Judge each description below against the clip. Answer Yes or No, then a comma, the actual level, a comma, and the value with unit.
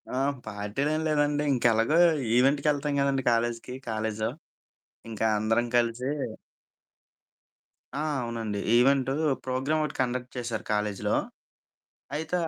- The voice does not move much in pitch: No, average, 3.7 semitones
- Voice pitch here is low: Yes, low, 125 Hz